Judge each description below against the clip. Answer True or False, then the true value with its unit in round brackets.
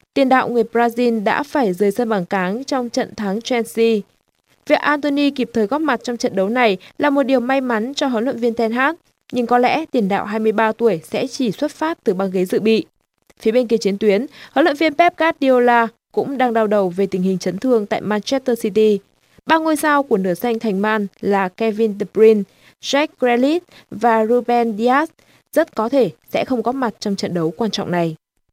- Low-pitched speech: False (235 Hz)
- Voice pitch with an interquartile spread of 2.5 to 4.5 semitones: True (4.0 semitones)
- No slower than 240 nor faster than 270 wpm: False (215 wpm)